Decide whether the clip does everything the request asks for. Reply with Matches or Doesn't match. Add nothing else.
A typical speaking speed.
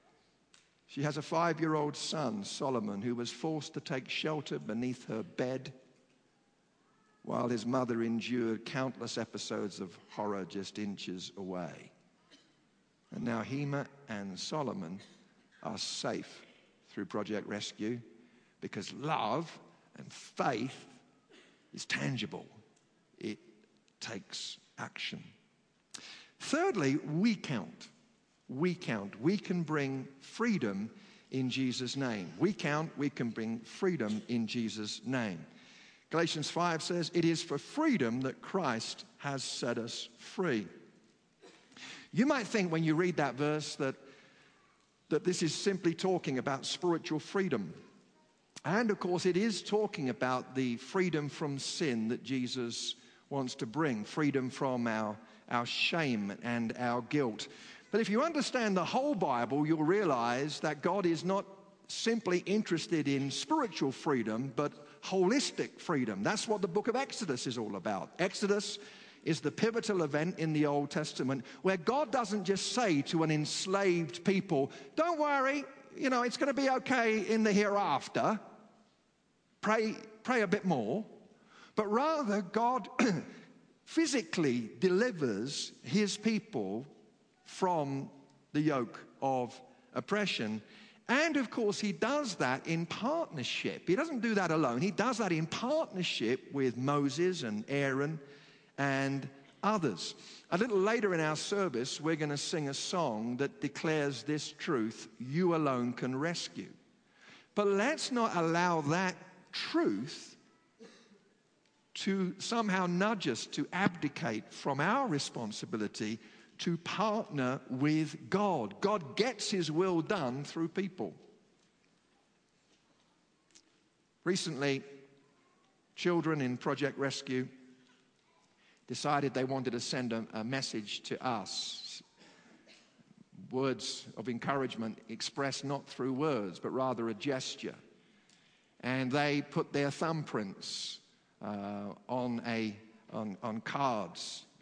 Doesn't match